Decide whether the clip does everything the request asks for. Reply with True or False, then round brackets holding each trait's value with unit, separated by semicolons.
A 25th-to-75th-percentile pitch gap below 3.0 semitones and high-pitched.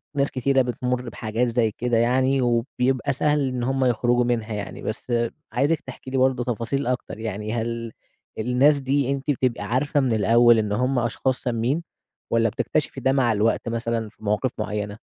False (2.5 semitones; 125 Hz)